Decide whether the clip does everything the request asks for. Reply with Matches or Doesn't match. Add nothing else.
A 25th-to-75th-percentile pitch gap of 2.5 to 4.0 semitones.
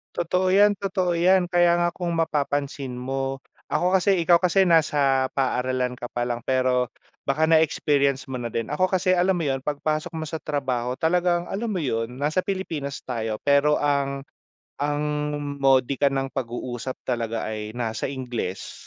Doesn't match